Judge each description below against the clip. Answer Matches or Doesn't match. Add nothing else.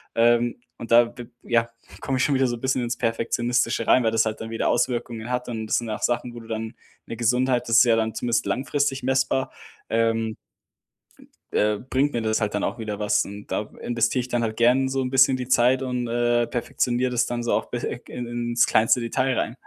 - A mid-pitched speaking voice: Doesn't match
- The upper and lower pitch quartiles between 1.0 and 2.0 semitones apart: Matches